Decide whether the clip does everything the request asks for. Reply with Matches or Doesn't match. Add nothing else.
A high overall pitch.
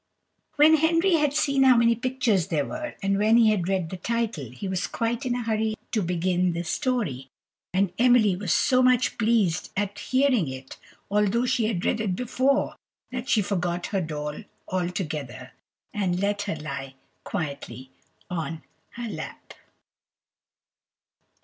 Matches